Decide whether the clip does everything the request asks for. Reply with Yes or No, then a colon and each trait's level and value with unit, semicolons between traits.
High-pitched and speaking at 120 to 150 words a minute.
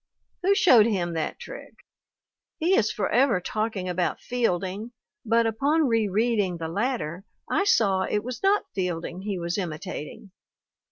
Yes: high, 210 Hz; average, 145 wpm